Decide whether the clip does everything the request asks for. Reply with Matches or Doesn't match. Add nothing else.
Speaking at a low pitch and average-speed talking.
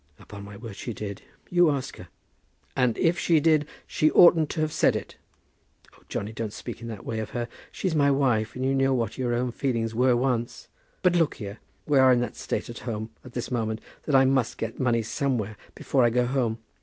Doesn't match